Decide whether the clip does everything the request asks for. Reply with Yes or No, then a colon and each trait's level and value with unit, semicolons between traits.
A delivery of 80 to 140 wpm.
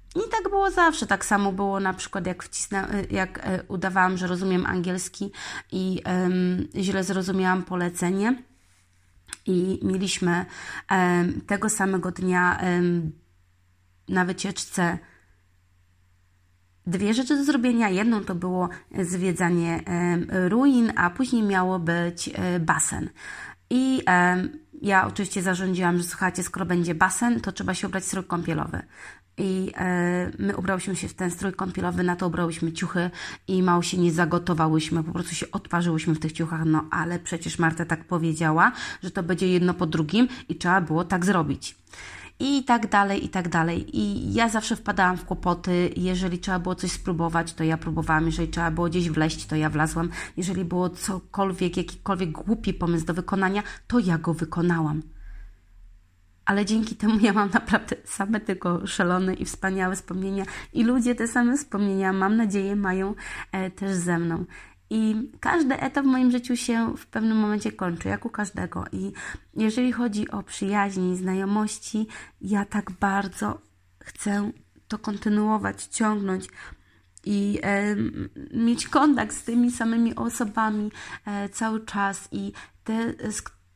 No: average, 150 wpm